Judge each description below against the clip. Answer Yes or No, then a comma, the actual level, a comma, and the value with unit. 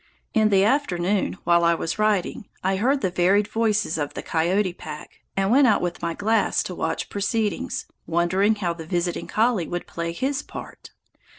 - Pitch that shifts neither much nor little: Yes, average, 3.8 semitones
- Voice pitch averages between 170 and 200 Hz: Yes, high, 190 Hz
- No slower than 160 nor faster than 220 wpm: Yes, average, 180 wpm